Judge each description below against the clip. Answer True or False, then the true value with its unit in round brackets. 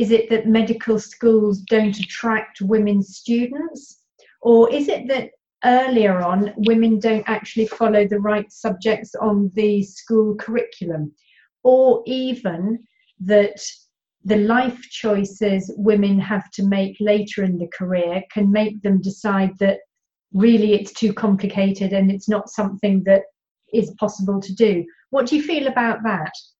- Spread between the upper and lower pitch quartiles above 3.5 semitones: False (2.5 semitones)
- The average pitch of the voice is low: False (210 Hz)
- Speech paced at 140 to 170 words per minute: True (145 wpm)